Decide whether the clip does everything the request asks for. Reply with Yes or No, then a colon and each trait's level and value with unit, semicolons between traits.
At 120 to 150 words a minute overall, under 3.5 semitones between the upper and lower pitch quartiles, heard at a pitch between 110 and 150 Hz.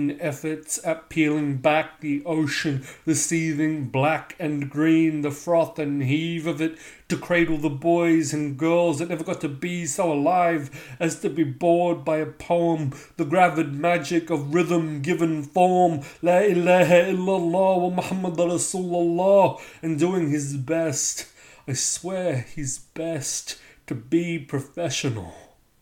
No: average, 140 wpm; narrow, 2.5 semitones; medium, 160 Hz